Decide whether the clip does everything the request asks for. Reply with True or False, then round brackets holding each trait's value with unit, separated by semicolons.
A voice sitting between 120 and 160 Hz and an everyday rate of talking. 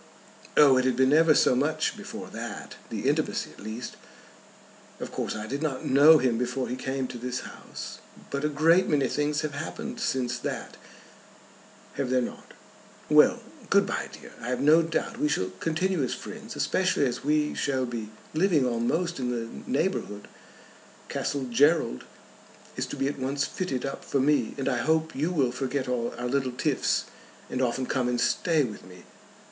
True (135 Hz; 180 wpm)